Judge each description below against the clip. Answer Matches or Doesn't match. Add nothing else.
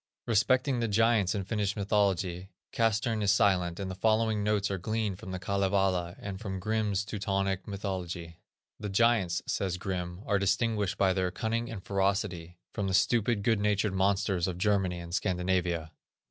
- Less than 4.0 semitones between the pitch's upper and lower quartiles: Matches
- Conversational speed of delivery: Matches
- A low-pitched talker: Matches